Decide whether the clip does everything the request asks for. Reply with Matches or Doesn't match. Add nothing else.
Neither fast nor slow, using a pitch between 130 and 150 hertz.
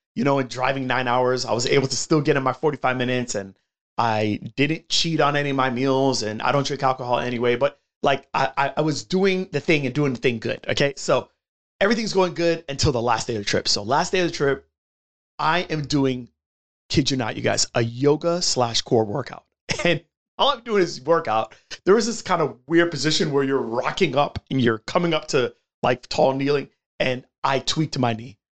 Doesn't match